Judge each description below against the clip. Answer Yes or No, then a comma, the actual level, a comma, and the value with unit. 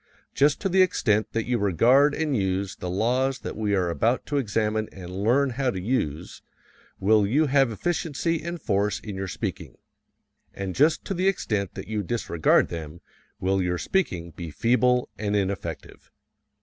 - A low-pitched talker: Yes, low, 110 Hz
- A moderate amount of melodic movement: No, wide, 6.1 semitones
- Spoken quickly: No, average, 170 wpm